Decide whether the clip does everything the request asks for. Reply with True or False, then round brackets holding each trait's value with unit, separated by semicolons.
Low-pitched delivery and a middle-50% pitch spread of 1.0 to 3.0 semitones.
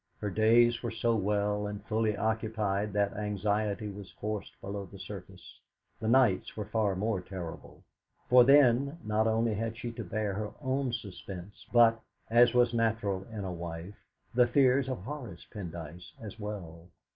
True (105 Hz; 2.7 semitones)